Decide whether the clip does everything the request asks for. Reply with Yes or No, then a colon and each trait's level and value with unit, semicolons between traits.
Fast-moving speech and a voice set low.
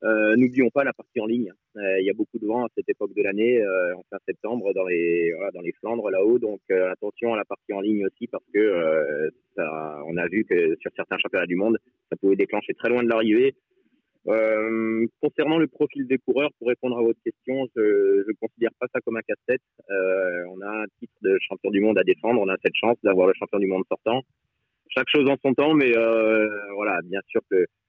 Yes: fast, 235 wpm; low, 125 Hz